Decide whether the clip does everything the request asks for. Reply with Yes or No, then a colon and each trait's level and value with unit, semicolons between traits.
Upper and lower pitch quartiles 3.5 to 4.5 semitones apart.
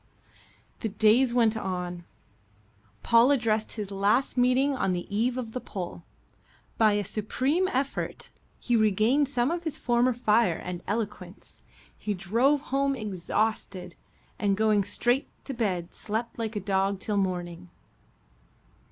Yes: average, 4.2 semitones